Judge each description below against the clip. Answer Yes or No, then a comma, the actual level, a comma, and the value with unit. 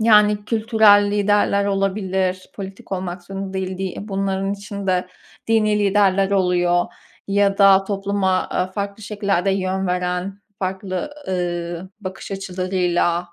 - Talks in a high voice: Yes, high, 195 Hz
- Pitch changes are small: Yes, narrow, 1.5 semitones